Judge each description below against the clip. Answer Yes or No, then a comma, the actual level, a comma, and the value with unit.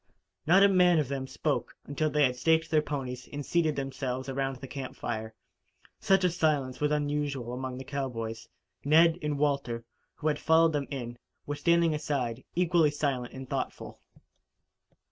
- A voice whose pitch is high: No, medium, 145 Hz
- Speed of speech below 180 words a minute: Yes, average, 165 wpm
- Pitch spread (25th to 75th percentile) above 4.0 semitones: No, average, 3.2 semitones